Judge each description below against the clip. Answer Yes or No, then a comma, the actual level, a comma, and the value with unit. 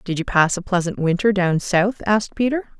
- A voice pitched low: No, high, 190 Hz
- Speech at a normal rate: No, fast, 215 wpm